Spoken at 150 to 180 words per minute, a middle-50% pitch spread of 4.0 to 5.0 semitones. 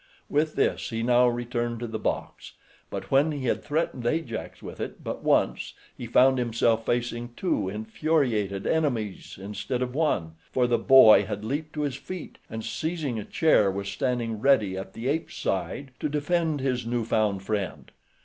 Yes: average, 175 wpm; average, 4.6 semitones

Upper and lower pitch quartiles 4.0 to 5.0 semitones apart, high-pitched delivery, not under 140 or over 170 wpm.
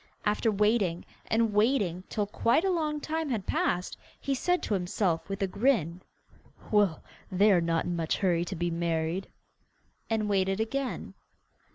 Yes: average, 4.6 semitones; high, 200 Hz; average, 160 wpm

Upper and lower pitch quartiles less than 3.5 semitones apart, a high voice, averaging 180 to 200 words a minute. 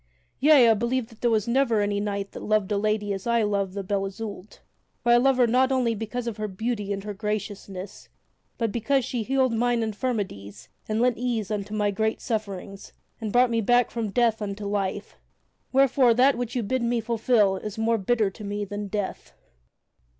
Yes: average, 2.9 semitones; high, 220 Hz; average, 195 wpm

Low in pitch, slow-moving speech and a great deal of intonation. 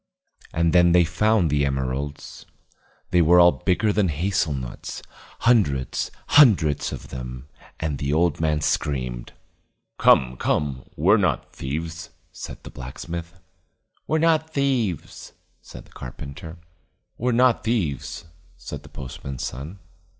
Yes: very low, 80 Hz; slow, 130 wpm; wide, 5.9 semitones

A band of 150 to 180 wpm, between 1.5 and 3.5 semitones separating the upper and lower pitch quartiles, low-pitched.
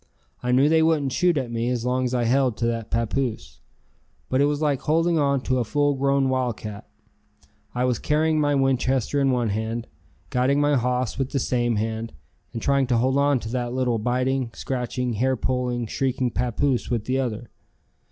No: average, 190 wpm; narrow, 2.5 semitones; low, 125 Hz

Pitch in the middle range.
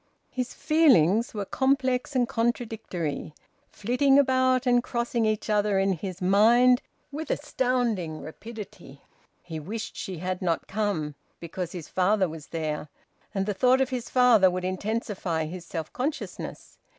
No: high, 210 Hz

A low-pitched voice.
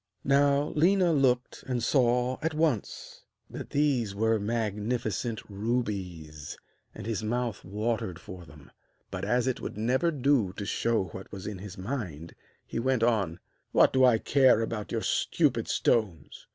Yes: low, 115 Hz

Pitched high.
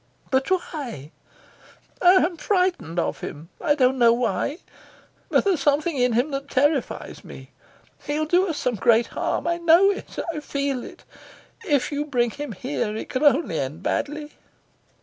Yes: very high, 280 Hz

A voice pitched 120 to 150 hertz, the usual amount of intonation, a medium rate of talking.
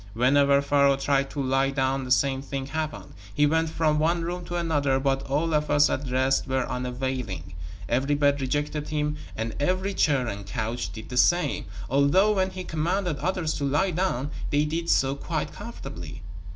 Yes: medium, 140 Hz; average, 3.1 semitones; average, 180 wpm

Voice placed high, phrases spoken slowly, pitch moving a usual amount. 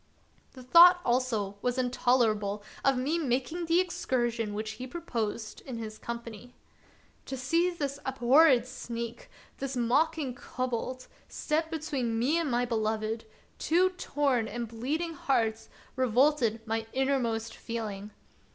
Yes: very high, 250 Hz; slow, 130 wpm; average, 4.1 semitones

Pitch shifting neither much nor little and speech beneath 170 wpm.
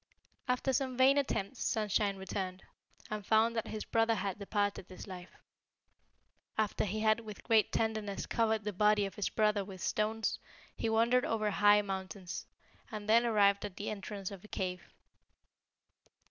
No: narrow, 2.1 semitones; average, 160 wpm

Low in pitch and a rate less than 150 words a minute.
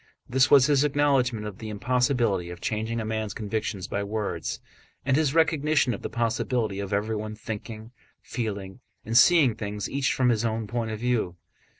No: low, 115 Hz; average, 175 wpm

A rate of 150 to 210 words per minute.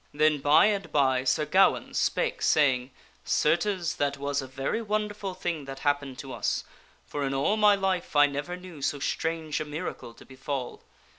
Yes: average, 180 wpm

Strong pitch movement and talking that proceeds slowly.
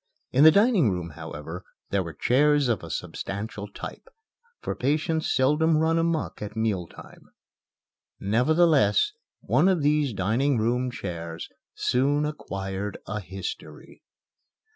Yes: wide, 7.5 semitones; slow, 125 wpm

